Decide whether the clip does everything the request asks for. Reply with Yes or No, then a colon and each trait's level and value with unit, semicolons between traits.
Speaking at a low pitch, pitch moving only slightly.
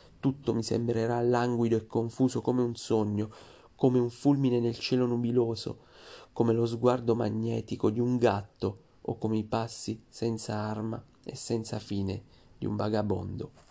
Yes: low, 115 Hz; narrow, 1.9 semitones